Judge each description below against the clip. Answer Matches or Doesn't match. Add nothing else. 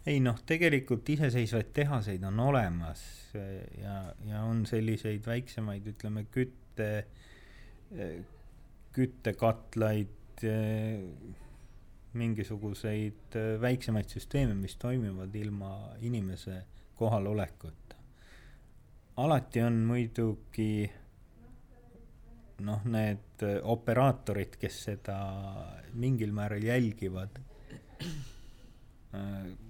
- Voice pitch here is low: Matches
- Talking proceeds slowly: Matches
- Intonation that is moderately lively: Matches